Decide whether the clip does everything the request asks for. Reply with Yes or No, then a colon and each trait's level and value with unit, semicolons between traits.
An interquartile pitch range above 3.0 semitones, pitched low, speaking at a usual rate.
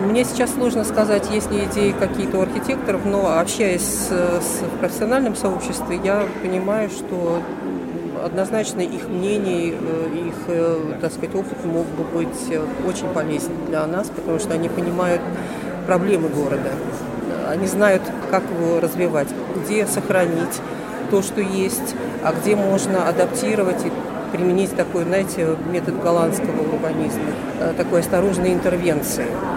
No: average, 3.4 semitones; high, 190 Hz; average, 130 wpm